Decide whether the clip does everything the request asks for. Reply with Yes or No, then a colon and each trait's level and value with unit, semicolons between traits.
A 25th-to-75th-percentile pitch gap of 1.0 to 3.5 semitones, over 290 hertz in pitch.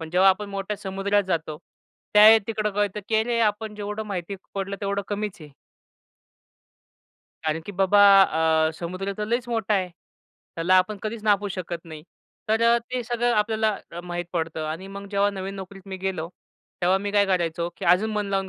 No: narrow, 2.6 semitones; high, 200 Hz